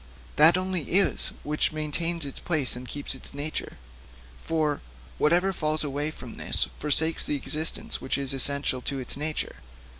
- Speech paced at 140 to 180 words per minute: Yes, average, 150 wpm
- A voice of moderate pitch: Yes, medium, 150 Hz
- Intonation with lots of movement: No, narrow, 2.5 semitones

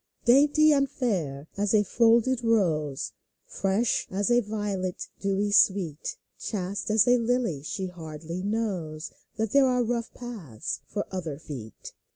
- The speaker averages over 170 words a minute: No, average, 140 wpm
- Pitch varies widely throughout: Yes, wide, 5.9 semitones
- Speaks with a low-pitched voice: No, high, 205 Hz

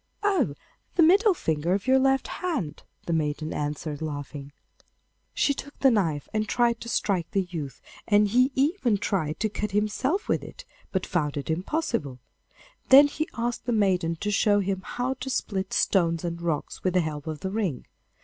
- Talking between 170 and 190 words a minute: Yes, average, 180 wpm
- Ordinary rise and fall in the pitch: No, wide, 7.5 semitones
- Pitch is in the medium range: No, high, 195 Hz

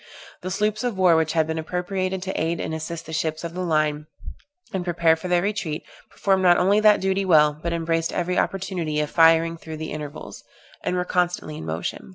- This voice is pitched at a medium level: Yes, medium, 170 Hz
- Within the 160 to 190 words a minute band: No, fast, 205 wpm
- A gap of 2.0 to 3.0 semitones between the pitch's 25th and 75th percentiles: Yes, average, 2.7 semitones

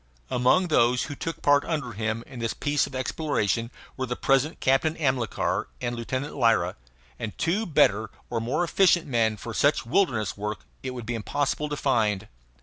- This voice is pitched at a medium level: No, low, 125 Hz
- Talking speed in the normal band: Yes, average, 175 wpm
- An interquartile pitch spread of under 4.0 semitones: No, average, 4.3 semitones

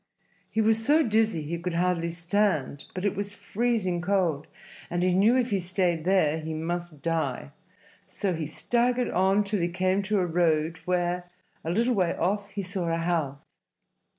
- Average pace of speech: Yes, average, 180 wpm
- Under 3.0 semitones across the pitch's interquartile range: No, average, 3.4 semitones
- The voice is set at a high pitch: No, medium, 180 Hz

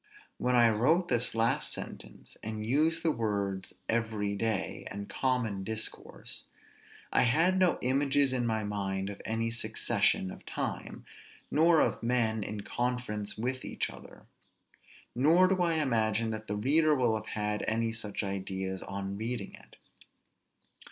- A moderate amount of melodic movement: Yes, average, 3.9 semitones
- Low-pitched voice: Yes, low, 115 Hz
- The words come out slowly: No, average, 145 wpm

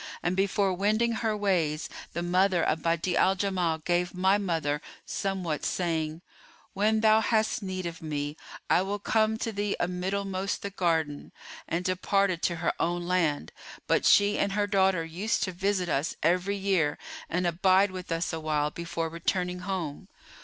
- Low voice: No, medium, 180 Hz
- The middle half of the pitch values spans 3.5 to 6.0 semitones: No, average, 3.1 semitones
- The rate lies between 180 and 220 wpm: No, average, 165 wpm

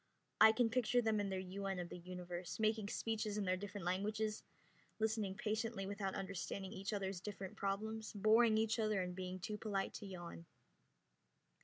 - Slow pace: No, average, 170 wpm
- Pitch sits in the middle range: No, high, 200 Hz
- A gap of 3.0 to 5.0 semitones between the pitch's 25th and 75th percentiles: No, narrow, 2.5 semitones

